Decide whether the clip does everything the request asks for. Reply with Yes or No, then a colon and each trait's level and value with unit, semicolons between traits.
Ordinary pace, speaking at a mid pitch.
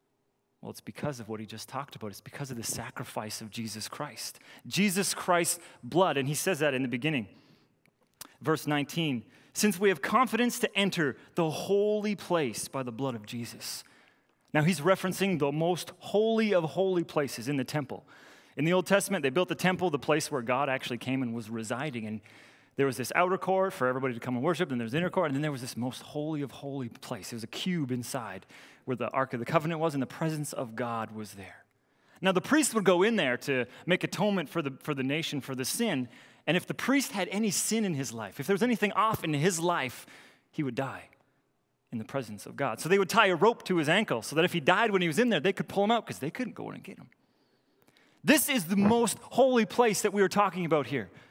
No: fast, 240 wpm; medium, 155 Hz